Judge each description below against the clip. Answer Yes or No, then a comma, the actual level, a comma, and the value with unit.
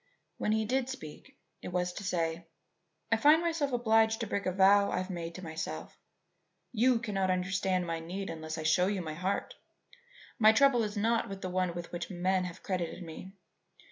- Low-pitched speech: No, high, 190 Hz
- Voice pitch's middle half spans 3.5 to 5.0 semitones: Yes, average, 4.2 semitones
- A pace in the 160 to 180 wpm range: No, average, 190 wpm